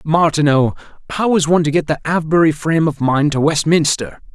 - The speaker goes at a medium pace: Yes, average, 180 wpm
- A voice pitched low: No, medium, 155 Hz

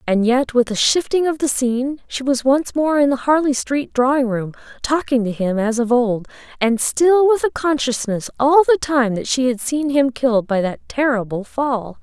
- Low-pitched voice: No, very high, 260 Hz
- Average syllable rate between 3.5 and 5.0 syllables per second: Yes, 4.7 syllables/s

